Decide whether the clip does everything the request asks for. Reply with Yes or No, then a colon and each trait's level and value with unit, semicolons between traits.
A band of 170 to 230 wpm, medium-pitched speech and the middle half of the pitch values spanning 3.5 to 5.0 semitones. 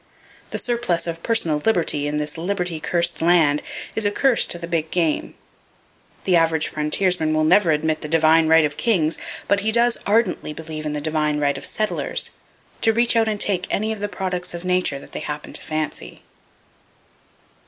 Yes: average, 185 wpm; medium, 170 Hz; average, 4.6 semitones